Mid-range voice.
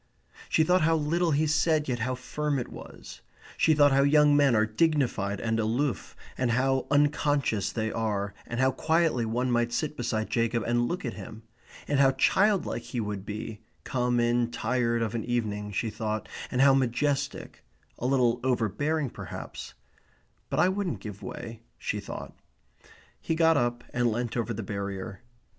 No: low, 120 Hz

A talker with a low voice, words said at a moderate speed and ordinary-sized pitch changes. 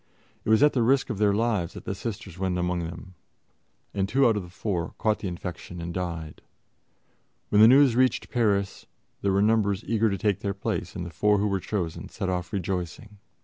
No: low, 100 Hz; fast, 210 wpm; average, 3.6 semitones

